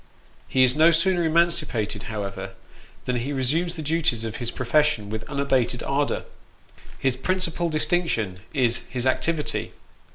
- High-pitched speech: No, low, 135 Hz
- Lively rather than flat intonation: Yes, wide, 5.8 semitones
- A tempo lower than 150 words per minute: Yes, average, 140 wpm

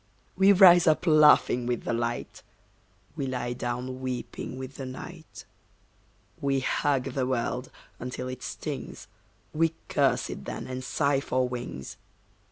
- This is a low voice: Yes, low, 130 Hz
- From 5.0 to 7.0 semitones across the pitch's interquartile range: No, average, 2.9 semitones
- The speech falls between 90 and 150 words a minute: Yes, average, 140 wpm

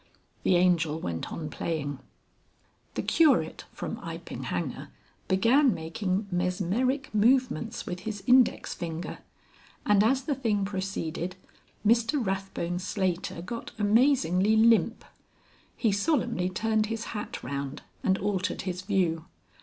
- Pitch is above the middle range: Yes, high, 195 Hz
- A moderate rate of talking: No, slow, 120 wpm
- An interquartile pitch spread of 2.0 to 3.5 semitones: No, average, 4.3 semitones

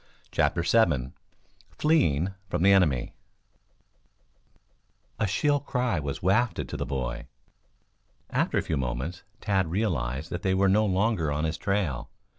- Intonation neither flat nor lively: No, wide, 6.2 semitones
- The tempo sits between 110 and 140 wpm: Yes, slow, 135 wpm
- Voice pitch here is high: No, very low, 90 Hz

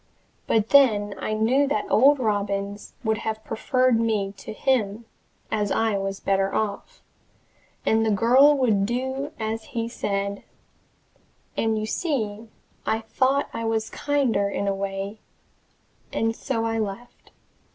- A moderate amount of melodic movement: Yes, average, 3.2 semitones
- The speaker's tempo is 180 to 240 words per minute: No, average, 140 wpm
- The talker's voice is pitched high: Yes, high, 220 Hz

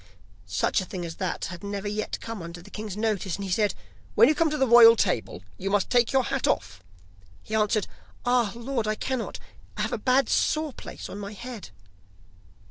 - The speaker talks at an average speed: No, fast, 210 wpm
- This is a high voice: Yes, high, 215 Hz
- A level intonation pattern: No, average, 3.9 semitones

